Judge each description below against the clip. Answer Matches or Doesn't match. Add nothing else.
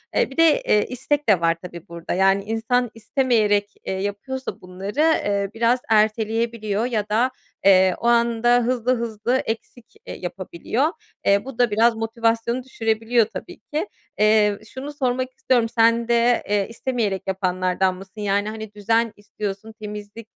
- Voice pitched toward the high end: Matches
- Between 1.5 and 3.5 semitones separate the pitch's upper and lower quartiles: Matches